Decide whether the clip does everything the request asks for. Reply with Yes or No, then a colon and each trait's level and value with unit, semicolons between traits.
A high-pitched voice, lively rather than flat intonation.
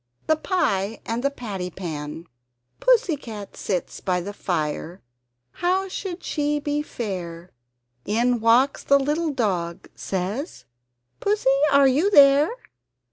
Yes: high, 245 Hz; wide, 8.0 semitones